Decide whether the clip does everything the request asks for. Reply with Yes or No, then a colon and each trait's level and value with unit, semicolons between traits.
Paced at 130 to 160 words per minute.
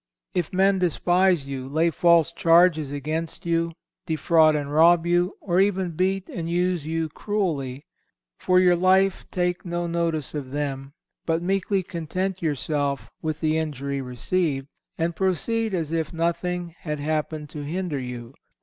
Yes: average, 150 wpm